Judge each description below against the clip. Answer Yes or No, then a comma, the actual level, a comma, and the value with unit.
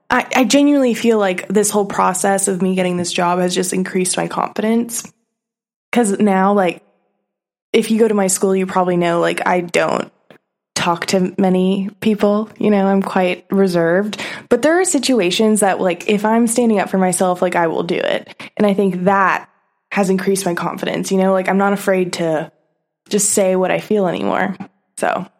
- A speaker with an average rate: Yes, average, 190 wpm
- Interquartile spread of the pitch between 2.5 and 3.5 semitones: Yes, average, 2.8 semitones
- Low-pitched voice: No, high, 195 Hz